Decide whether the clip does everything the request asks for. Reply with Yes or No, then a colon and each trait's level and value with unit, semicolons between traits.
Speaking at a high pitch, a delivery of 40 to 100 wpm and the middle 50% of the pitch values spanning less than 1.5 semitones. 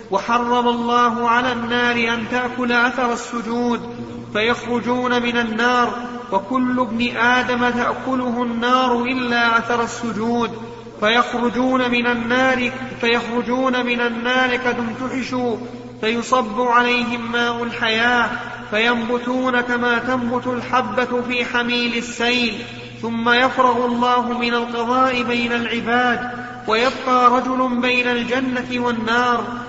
Yes: high, 240 Hz; average, 95 wpm; narrow, 0.7 semitones